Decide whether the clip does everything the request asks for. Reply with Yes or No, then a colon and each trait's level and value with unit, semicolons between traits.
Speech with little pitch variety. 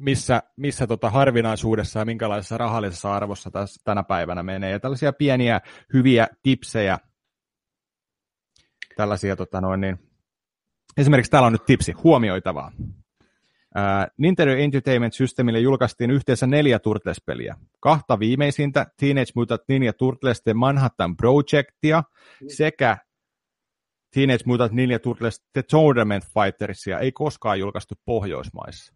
No: average, 4.6 semitones